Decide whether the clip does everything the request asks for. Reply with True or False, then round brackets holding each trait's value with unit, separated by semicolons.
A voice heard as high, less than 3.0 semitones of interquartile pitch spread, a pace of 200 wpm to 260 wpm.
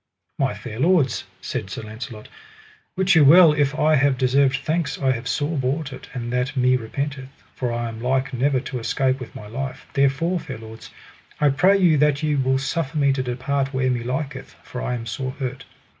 False (135 Hz; 2.5 semitones; 205 wpm)